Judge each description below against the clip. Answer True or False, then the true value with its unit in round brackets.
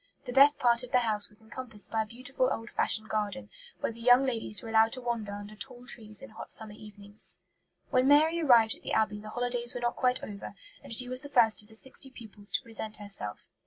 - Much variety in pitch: False (2.8 semitones)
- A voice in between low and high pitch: False (230 Hz)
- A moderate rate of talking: False (235 wpm)